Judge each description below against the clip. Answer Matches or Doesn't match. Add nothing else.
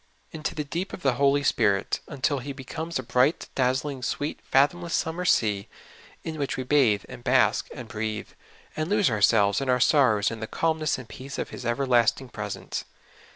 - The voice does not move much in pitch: Doesn't match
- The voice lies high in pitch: Doesn't match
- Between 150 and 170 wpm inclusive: Doesn't match